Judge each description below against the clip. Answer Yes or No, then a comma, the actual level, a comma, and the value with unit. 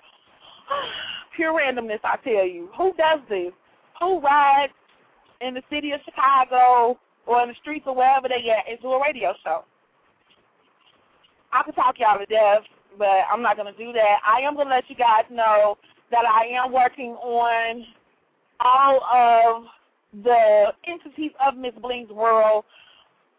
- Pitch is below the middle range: No, very high, 250 Hz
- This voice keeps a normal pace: Yes, average, 150 wpm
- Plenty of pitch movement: No, average, 4.3 semitones